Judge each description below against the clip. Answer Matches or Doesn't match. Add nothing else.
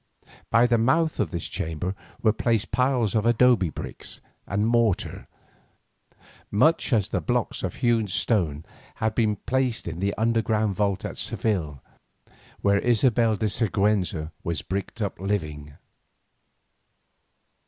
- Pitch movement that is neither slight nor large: Matches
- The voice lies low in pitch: Matches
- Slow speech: Matches